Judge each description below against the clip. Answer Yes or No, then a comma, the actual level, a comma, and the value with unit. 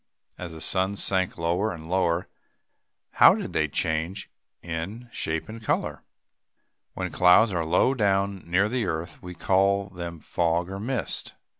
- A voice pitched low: Yes, very low, 95 Hz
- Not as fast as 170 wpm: Yes, average, 150 wpm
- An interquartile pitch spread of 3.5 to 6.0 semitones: No, average, 2.9 semitones